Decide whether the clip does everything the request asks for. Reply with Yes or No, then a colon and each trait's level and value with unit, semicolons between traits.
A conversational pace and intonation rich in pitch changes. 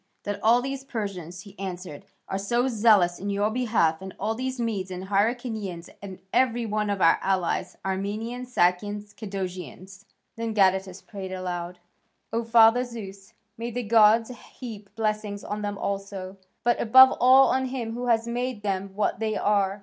No: average, 165 wpm; average, 3.3 semitones